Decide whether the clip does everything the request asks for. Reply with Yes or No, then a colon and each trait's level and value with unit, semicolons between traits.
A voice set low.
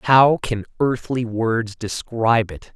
Yes: low, 115 Hz